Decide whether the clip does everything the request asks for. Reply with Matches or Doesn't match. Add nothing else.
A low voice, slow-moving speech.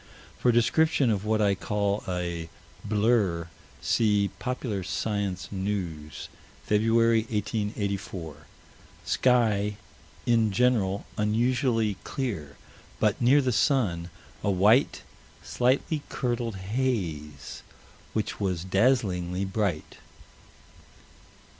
Matches